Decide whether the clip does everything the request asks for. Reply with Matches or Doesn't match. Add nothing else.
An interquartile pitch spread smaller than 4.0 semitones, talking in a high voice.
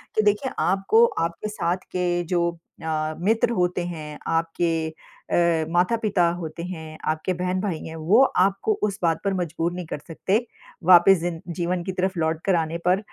Doesn't match